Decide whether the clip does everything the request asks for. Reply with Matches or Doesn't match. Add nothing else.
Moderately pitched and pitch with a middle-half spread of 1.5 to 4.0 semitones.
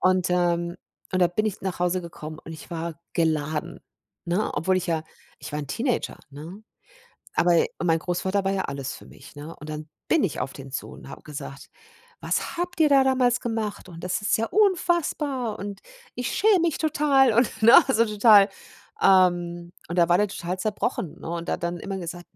Doesn't match